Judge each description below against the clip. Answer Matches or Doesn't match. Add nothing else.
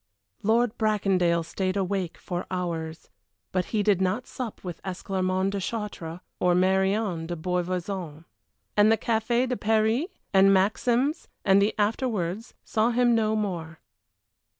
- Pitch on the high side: Matches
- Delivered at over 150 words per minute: Doesn't match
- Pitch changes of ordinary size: Matches